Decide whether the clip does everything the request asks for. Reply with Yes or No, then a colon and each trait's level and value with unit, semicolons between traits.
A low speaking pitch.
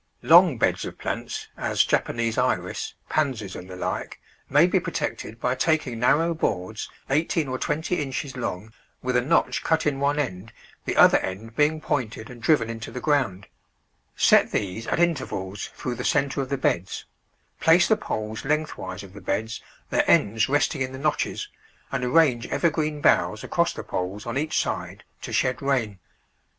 Yes: low, 130 Hz